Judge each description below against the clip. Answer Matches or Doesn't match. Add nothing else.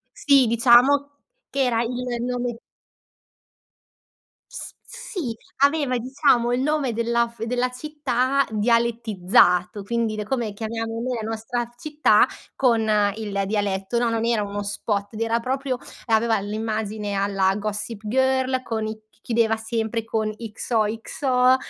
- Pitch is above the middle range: Matches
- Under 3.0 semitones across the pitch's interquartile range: Matches